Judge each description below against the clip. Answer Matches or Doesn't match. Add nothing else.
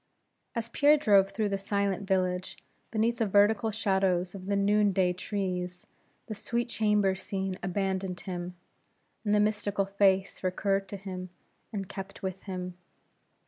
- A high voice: Matches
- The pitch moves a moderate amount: Doesn't match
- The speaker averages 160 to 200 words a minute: Doesn't match